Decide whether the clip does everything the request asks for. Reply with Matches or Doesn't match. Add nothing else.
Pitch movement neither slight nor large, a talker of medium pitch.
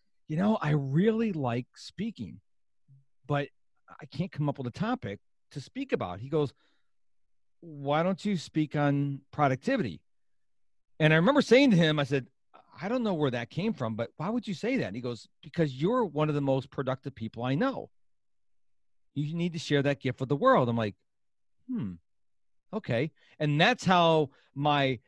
Doesn't match